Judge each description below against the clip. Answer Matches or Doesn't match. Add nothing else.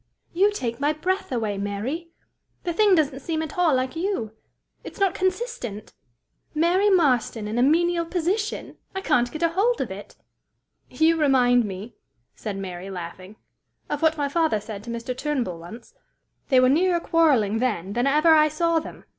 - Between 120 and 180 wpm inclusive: Matches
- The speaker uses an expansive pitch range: Matches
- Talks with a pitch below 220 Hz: Doesn't match